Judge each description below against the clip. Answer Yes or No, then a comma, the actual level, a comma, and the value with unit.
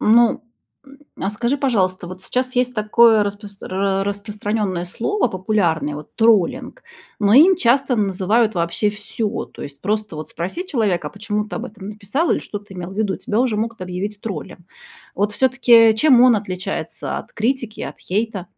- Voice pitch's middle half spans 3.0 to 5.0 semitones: Yes, average, 3.6 semitones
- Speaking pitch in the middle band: No, high, 210 Hz